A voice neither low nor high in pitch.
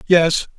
Yes: medium, 170 Hz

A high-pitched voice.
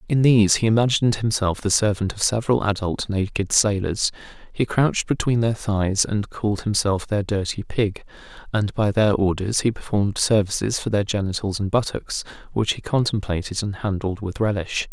No: low, 105 Hz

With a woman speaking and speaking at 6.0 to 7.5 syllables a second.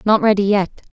Yes: female; 6.4 syllables/s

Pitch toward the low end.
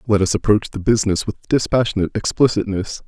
Yes: low, 105 Hz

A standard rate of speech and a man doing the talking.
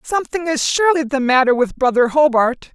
No: average, 175 wpm; female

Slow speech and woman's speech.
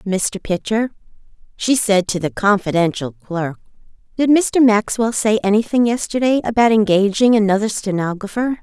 Yes: slow, 125 wpm; female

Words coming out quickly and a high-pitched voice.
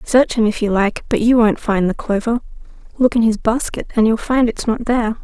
Yes: fast, 240 wpm; high, 225 Hz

